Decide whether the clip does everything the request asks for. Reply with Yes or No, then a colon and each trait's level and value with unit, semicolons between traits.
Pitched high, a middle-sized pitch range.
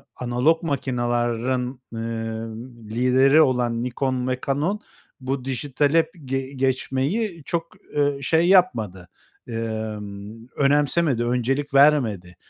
No: low, 130 Hz; average, 3.7 semitones